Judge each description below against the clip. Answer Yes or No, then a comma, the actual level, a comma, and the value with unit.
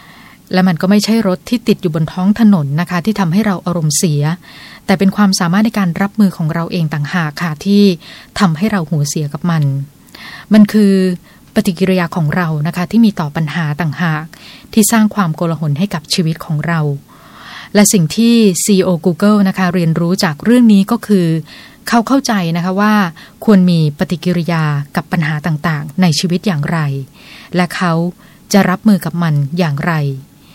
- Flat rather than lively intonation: No, average, 3.7 semitones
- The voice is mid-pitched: Yes, medium, 180 Hz